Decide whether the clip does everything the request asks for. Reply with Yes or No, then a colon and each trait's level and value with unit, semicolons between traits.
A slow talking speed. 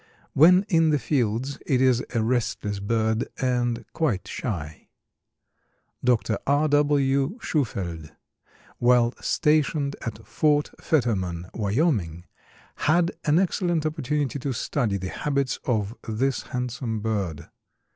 Yes: slow, 115 wpm